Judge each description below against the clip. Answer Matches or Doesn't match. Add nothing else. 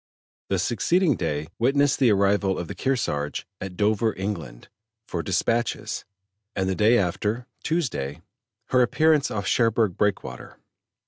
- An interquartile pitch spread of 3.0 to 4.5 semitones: Doesn't match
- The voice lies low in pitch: Matches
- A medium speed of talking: Doesn't match